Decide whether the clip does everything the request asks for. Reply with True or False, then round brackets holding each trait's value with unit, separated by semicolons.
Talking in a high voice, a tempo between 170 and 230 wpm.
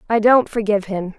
True (210 Hz; 200 wpm)